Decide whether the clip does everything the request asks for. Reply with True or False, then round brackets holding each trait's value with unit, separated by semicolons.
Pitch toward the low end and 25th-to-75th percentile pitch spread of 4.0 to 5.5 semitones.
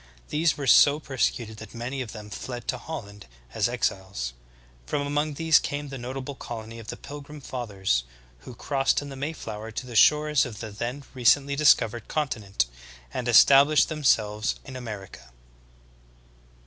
True (125 Hz; 4.7 semitones)